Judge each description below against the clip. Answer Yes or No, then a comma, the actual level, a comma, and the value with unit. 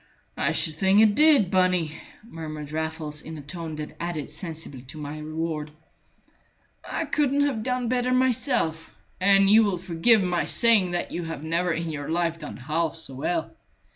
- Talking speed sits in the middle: Yes, average, 170 wpm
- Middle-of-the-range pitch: Yes, medium, 170 Hz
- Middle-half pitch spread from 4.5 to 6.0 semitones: Yes, average, 4.8 semitones